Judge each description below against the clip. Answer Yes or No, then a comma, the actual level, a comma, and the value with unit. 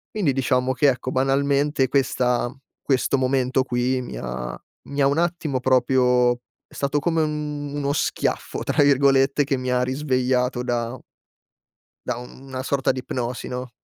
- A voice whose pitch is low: Yes, low, 130 Hz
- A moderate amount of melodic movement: No, narrow, 2.0 semitones